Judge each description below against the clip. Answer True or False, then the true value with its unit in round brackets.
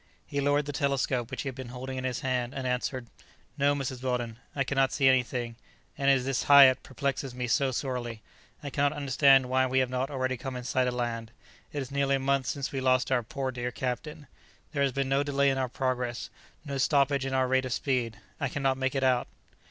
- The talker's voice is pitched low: True (130 Hz)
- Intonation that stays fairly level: True (1.6 semitones)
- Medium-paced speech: False (230 wpm)